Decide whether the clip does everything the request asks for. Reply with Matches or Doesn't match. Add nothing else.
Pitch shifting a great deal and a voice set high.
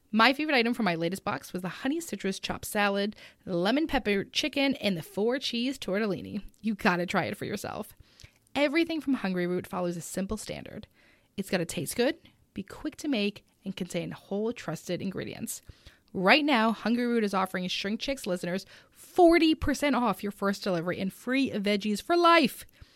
Matches